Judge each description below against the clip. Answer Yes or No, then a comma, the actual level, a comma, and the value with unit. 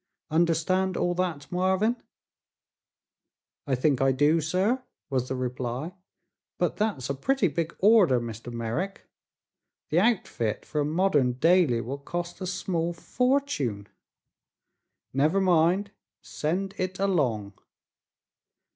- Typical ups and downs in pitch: No, wide, 6.1 semitones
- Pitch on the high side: No, medium, 165 Hz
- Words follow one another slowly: Yes, slow, 115 wpm